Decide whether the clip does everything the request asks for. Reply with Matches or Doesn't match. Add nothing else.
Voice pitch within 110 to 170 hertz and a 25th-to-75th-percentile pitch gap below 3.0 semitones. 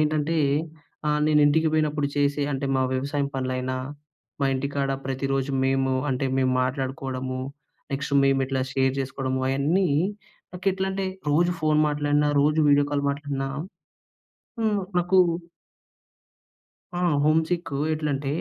Matches